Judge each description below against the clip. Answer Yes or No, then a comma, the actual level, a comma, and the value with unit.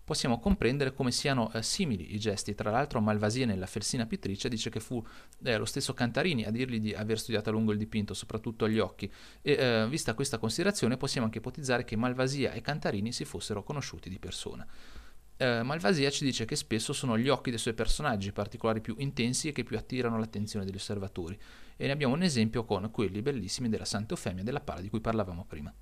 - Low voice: Yes, low, 115 Hz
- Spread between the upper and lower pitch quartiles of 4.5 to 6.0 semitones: No, average, 3.2 semitones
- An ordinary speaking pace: No, fast, 205 wpm